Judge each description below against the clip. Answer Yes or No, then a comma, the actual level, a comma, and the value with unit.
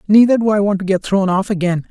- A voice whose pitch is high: Yes, high, 200 Hz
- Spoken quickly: Yes, fast, 285 wpm